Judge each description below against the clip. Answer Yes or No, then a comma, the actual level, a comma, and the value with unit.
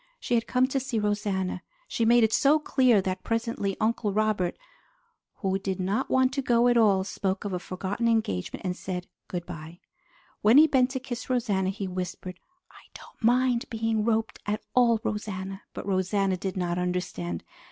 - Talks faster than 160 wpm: Yes, average, 180 wpm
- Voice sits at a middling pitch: No, high, 210 Hz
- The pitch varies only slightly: No, average, 3.9 semitones